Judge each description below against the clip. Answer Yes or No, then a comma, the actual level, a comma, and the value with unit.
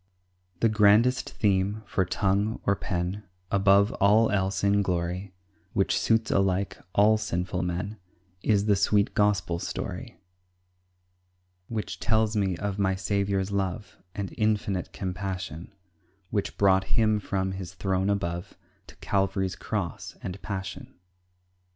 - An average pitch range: No, narrow, 1.7 semitones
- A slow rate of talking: Yes, slow, 125 wpm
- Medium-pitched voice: No, low, 100 Hz